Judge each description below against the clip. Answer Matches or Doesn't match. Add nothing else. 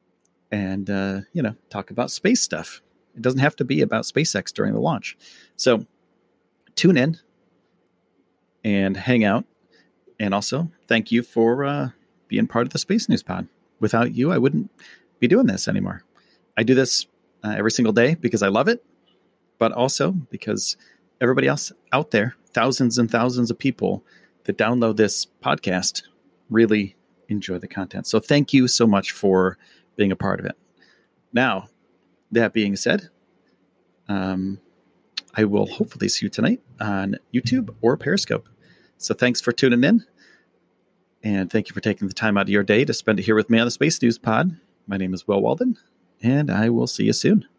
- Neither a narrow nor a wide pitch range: Matches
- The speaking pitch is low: Matches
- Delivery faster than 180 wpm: Doesn't match